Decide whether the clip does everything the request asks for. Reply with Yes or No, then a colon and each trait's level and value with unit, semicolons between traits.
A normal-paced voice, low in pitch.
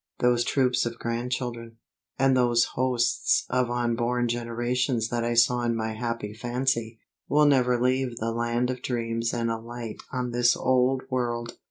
Yes: average, 155 wpm; low, 120 Hz